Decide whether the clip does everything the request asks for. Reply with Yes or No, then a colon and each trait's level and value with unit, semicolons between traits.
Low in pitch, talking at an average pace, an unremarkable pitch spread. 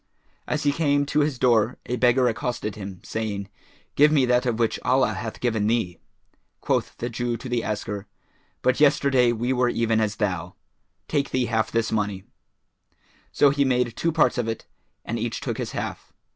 Yes: low, 120 Hz; average, 185 wpm; average, 3.0 semitones